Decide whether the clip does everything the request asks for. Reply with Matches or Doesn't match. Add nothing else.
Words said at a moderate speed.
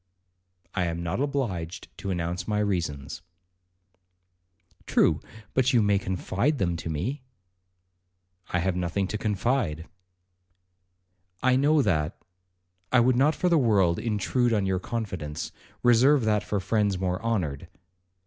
Doesn't match